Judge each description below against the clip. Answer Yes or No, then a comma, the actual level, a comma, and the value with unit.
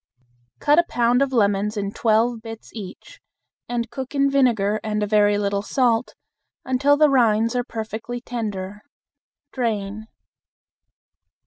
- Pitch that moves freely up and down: No, average, 3.2 semitones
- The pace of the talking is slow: Yes, slow, 130 wpm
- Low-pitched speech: No, high, 225 Hz